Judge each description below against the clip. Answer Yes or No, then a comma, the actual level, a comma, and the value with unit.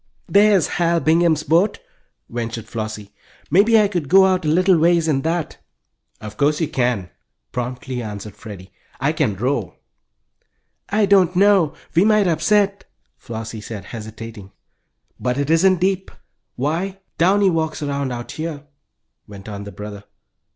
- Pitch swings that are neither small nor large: No, wide, 8.2 semitones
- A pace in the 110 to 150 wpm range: Yes, average, 145 wpm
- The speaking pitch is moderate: Yes, medium, 155 Hz